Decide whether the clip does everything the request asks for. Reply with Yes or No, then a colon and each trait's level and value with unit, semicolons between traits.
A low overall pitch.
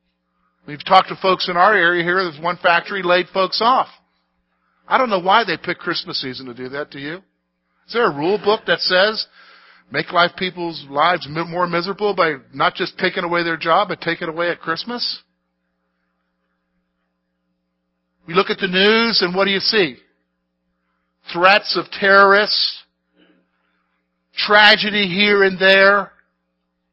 No: medium, 170 Hz